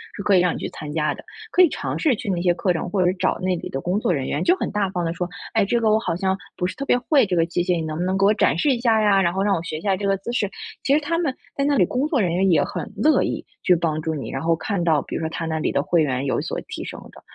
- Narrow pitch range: No, average, 4.6 semitones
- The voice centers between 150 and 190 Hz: Yes, medium, 185 Hz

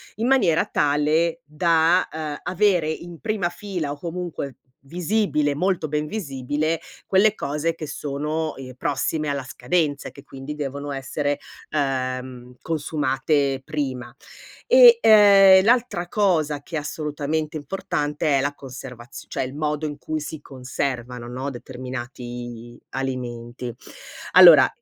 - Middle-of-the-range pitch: Yes, medium, 150 Hz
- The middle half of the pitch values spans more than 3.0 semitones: Yes, average, 3.8 semitones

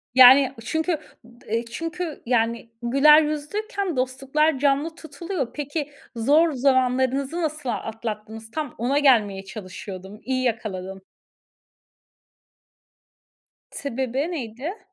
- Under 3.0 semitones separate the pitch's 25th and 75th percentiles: No, average, 4.8 semitones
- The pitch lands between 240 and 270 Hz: Yes, very high, 265 Hz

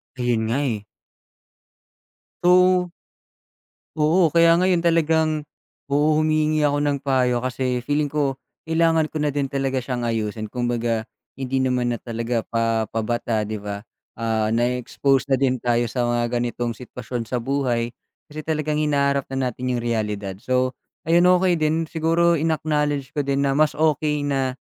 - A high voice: No, low, 135 Hz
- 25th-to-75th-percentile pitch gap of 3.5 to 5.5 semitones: Yes, average, 4.2 semitones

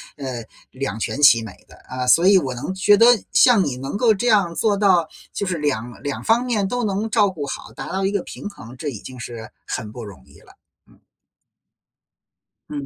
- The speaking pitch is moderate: Yes, medium, 165 Hz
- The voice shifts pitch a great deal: Yes, wide, 8.2 semitones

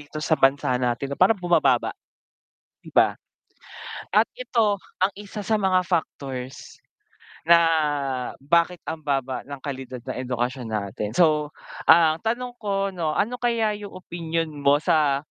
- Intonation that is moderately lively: No, wide, 6.1 semitones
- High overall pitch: No, medium, 160 Hz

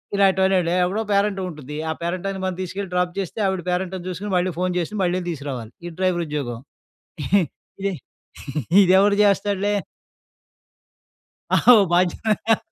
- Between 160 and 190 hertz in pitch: Yes, medium, 185 Hz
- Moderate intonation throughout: No, narrow, 2.2 semitones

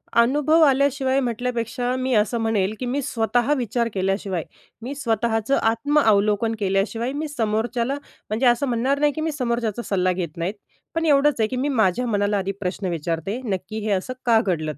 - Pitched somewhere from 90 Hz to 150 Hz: No, high, 230 Hz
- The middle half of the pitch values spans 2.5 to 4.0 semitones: No, average, 4.4 semitones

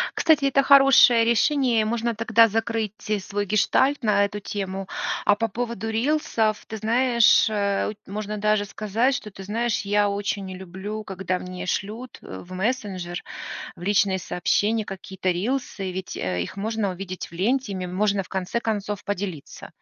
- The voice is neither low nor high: No, high, 210 Hz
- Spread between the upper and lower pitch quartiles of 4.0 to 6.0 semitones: No, average, 3.0 semitones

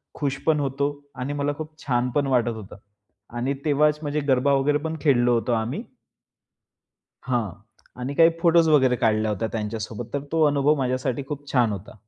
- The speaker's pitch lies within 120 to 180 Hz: Yes, low, 135 Hz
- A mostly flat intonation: No, average, 3.4 semitones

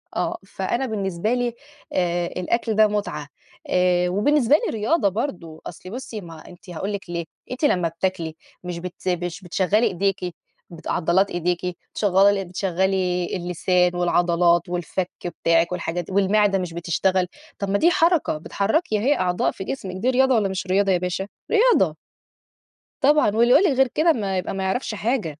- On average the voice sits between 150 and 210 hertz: Yes, high, 190 Hz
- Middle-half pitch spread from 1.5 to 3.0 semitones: No, average, 3.6 semitones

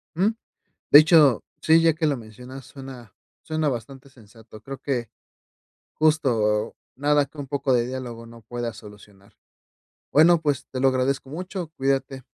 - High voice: No, low, 135 Hz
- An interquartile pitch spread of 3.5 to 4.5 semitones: Yes, average, 3.9 semitones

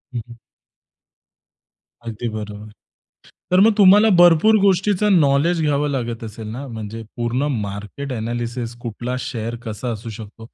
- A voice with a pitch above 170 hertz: No, low, 120 Hz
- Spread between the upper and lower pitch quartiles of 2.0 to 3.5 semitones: No, wide, 5.6 semitones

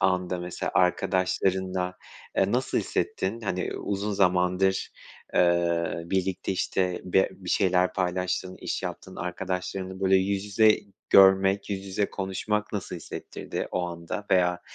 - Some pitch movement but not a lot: No, narrow, 1.1 semitones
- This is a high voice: No, very low, 95 Hz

